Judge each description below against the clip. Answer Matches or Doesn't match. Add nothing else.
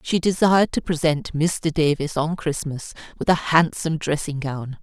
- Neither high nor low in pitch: Matches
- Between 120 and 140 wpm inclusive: Doesn't match